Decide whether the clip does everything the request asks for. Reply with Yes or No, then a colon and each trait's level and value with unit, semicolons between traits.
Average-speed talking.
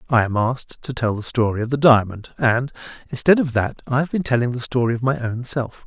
No: fast, 245 wpm